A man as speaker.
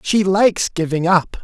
Yes: male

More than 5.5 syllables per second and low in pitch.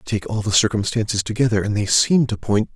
Yes: 5.8 syllables/s; low, 110 Hz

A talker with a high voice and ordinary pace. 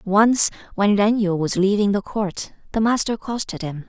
Yes: high, 205 Hz; average, 185 wpm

